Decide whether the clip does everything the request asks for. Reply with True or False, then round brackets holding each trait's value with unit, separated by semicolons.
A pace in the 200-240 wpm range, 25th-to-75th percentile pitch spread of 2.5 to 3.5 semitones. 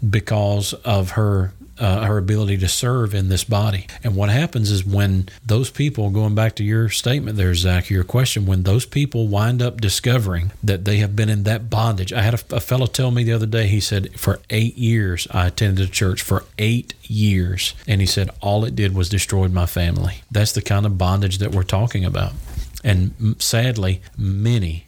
True (205 wpm; 2.9 semitones)